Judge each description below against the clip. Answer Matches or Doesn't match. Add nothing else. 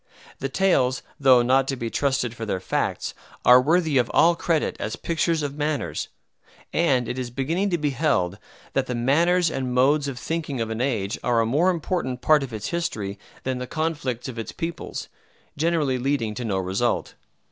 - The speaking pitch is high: Doesn't match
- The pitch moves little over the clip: Doesn't match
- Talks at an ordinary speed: Matches